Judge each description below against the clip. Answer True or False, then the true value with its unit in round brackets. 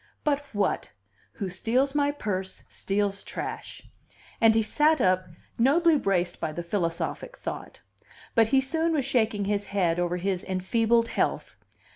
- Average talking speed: True (145 wpm)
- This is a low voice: False (210 Hz)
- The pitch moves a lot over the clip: True (6.4 semitones)